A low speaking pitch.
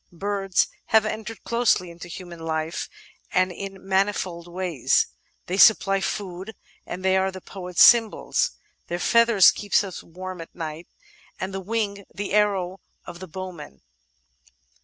No: high, 190 Hz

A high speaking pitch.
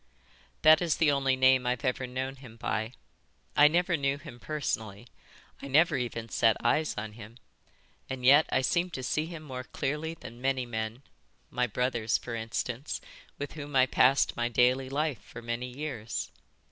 No: low, 130 Hz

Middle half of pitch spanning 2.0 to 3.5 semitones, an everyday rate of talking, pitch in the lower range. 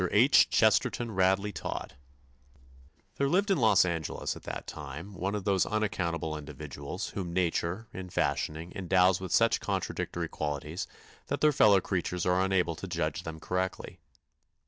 Yes: average, 2.8 semitones; average, 145 wpm; very low, 90 Hz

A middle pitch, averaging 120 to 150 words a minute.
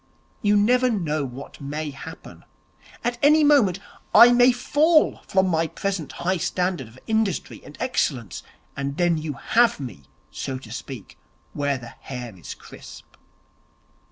Yes: medium, 170 Hz; average, 145 wpm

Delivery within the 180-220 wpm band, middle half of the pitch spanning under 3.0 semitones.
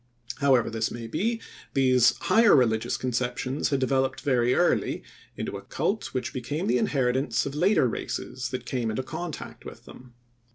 No: average, 160 wpm; narrow, 2.5 semitones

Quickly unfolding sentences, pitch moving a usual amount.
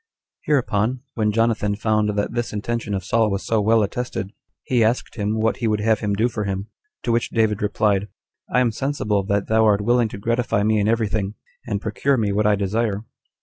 No: fast, 215 wpm; narrow, 2.0 semitones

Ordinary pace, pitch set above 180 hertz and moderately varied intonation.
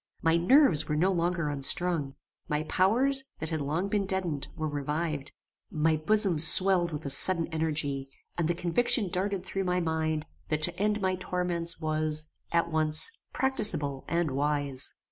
No: average, 160 wpm; medium, 165 Hz; average, 3.4 semitones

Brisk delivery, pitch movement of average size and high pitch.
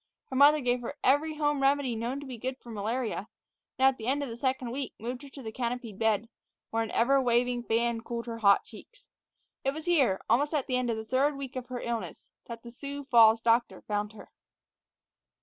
Yes: fast, 220 wpm; average, 3.0 semitones; high, 245 Hz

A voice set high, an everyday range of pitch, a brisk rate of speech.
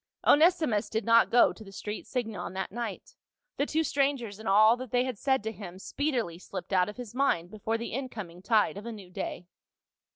Yes: high, 220 Hz; average, 4.2 semitones; fast, 215 wpm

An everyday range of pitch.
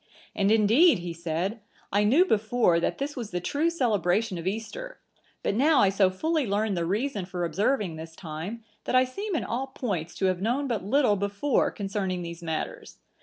No: wide, 6.2 semitones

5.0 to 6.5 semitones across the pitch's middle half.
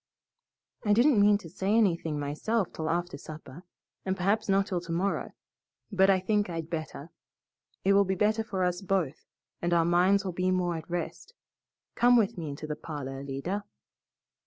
No: average, 3.4 semitones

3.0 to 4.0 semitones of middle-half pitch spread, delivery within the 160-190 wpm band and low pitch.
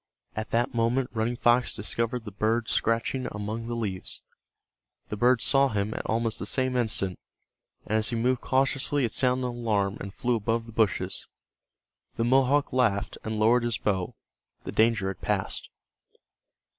No: narrow, 2.5 semitones; average, 165 wpm; low, 115 Hz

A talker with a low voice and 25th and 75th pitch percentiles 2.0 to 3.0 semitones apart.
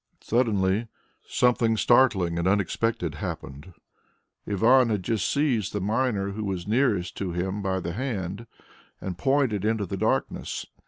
No: low, 105 Hz; average, 3.7 semitones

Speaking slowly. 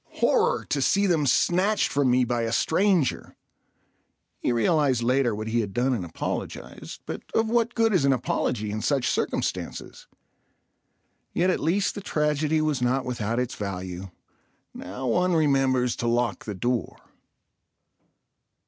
No: average, 150 wpm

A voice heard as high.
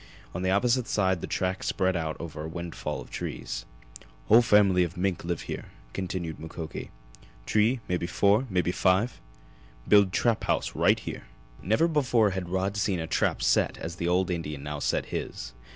No: very low, 95 Hz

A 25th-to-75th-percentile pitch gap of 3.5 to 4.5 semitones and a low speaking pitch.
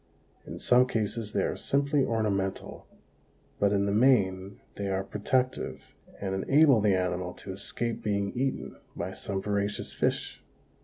Yes: average, 4.1 semitones; low, 105 Hz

